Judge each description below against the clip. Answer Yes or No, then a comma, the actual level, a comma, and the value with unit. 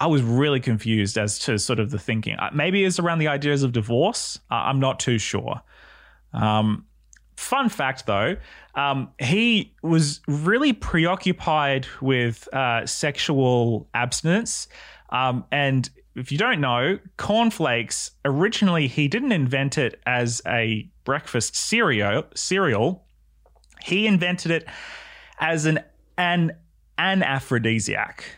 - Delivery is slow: Yes, slow, 125 wpm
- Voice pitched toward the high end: No, medium, 140 Hz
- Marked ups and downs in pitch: Yes, wide, 6.1 semitones